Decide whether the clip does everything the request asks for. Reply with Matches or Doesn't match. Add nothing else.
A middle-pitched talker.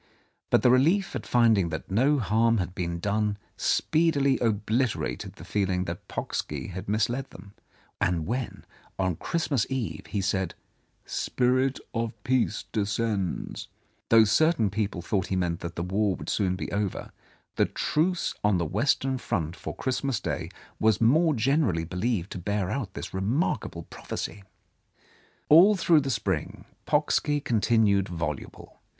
Doesn't match